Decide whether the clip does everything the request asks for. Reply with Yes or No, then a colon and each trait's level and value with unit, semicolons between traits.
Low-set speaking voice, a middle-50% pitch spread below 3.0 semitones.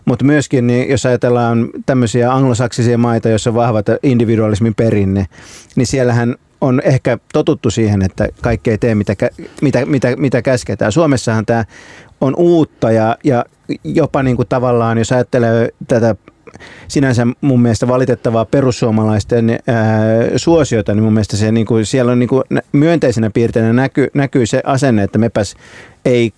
Yes: low, 120 Hz; narrow, 2.6 semitones